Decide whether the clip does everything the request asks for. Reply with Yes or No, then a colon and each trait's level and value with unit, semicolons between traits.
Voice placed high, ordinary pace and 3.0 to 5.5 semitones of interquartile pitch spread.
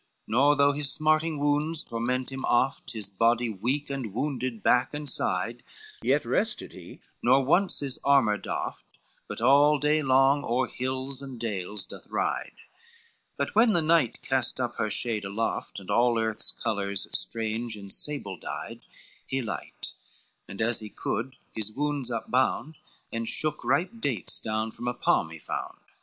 No: low, 125 Hz; average, 165 wpm; average, 4.2 semitones